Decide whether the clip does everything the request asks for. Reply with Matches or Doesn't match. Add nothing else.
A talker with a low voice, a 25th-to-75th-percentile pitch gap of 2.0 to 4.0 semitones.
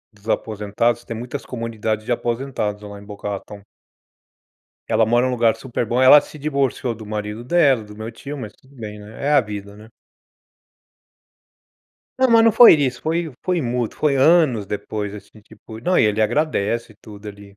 Doesn't match